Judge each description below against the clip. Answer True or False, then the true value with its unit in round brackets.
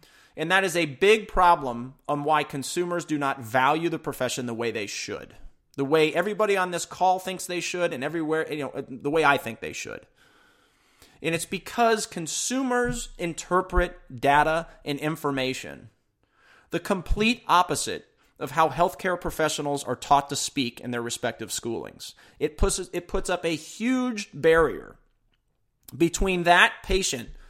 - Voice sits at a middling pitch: True (160 Hz)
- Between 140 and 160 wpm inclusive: True (155 wpm)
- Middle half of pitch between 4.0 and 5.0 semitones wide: True (4.7 semitones)